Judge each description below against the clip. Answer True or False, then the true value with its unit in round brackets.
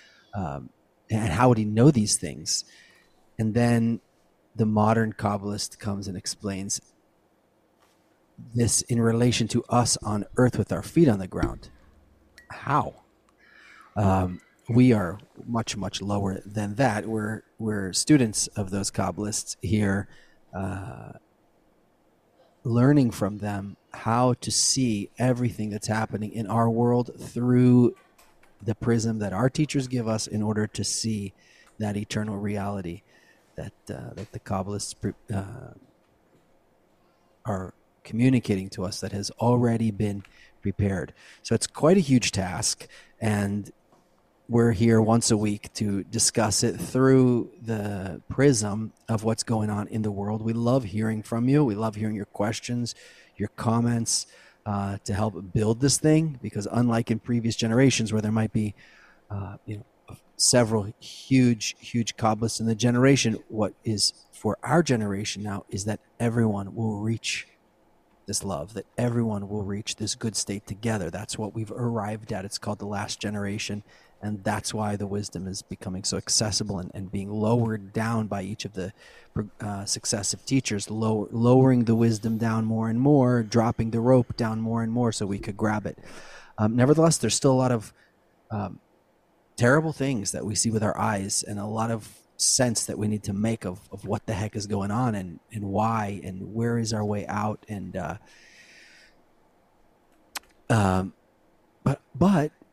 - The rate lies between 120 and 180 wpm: True (160 wpm)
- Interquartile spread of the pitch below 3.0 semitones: True (2.6 semitones)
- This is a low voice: True (110 Hz)